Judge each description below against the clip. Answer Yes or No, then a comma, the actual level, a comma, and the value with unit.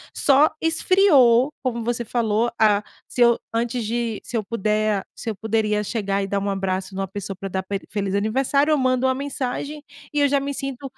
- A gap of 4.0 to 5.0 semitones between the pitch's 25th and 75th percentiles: Yes, average, 4.6 semitones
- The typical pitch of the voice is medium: No, high, 230 Hz